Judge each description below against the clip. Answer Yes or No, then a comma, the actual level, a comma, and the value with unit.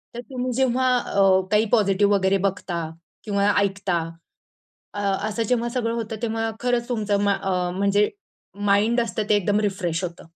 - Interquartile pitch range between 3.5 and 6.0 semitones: No, average, 2.8 semitones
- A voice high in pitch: Yes, high, 205 Hz